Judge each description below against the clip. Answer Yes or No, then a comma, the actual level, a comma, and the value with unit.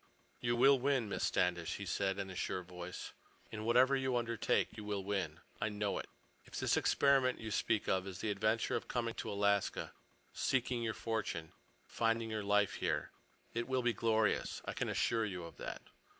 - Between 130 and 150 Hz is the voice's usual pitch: No, low, 110 Hz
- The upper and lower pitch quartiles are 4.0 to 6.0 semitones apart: No, average, 3.1 semitones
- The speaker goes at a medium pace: Yes, average, 180 wpm